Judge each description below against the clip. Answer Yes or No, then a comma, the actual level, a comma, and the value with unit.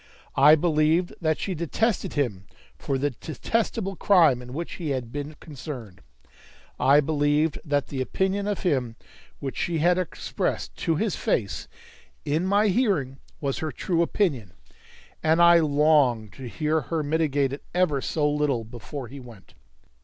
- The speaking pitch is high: No, medium, 150 Hz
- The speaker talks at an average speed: Yes, average, 155 wpm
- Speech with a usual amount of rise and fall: Yes, average, 4.1 semitones